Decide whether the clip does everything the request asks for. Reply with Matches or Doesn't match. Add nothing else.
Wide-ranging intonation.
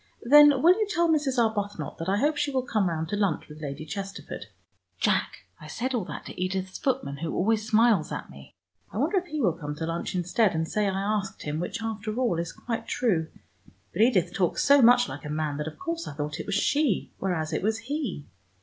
Matches